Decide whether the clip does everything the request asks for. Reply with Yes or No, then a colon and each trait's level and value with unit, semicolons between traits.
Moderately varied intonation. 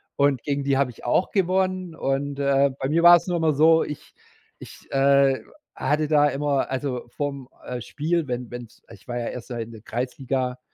Yes: average, 3.5 semitones